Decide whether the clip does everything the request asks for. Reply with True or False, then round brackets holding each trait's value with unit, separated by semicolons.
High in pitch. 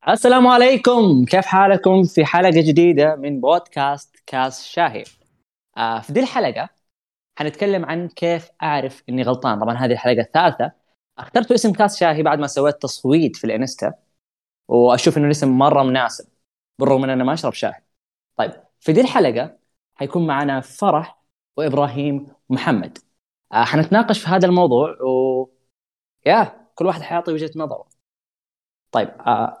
False (150 Hz)